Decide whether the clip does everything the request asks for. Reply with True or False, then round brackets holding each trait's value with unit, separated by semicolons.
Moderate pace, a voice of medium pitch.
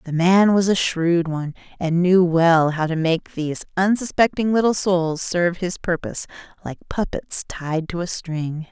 True (170 wpm; 175 Hz)